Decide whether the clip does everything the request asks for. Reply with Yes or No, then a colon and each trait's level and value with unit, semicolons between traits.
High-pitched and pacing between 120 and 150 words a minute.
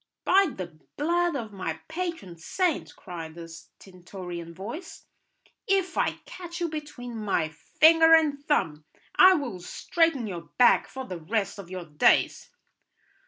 Yes: high, 225 Hz; average, 140 wpm